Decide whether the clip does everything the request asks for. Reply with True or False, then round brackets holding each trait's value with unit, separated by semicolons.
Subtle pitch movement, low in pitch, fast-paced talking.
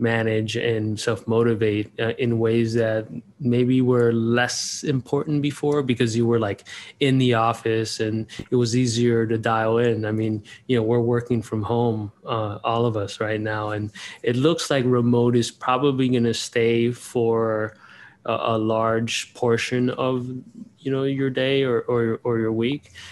False (1.9 semitones; 115 Hz; 170 wpm)